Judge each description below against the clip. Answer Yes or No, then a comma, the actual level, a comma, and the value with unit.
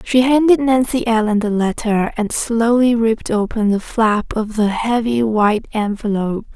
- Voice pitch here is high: Yes, high, 225 Hz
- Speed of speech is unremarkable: Yes, average, 155 wpm